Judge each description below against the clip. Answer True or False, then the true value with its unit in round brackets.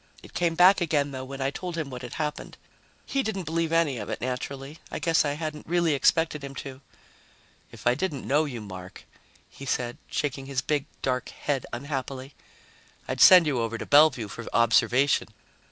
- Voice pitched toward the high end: False (140 Hz)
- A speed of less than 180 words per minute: False (185 wpm)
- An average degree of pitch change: True (3.7 semitones)